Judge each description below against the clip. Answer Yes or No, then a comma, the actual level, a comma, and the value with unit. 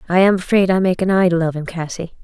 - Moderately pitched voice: Yes, medium, 180 Hz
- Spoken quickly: Yes, fast, 270 wpm